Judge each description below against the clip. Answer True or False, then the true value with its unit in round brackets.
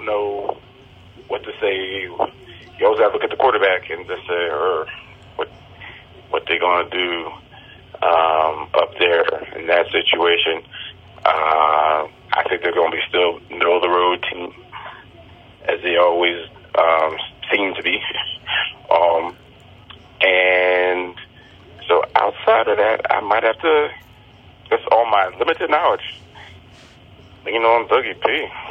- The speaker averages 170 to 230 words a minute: False (140 wpm)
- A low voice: True (90 Hz)